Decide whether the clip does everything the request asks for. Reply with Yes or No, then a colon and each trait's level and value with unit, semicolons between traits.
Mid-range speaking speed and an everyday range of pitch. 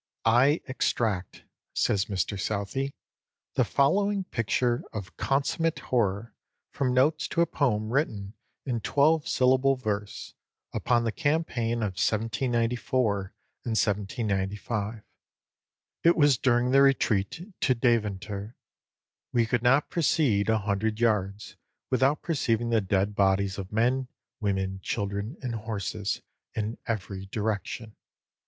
No: slow, 120 wpm; average, 4.3 semitones